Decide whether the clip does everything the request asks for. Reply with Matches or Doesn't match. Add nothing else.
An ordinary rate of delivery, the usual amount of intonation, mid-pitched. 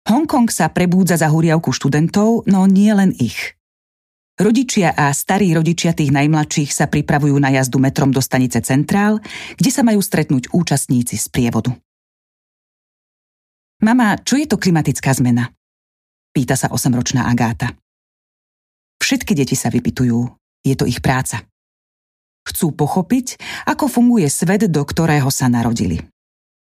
Doesn't match